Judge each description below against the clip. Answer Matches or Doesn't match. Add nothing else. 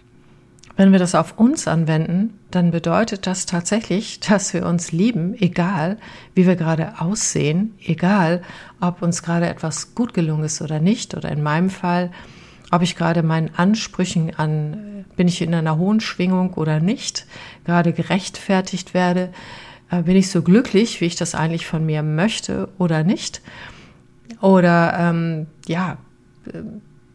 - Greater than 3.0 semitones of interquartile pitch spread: Doesn't match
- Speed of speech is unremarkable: Matches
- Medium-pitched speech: Matches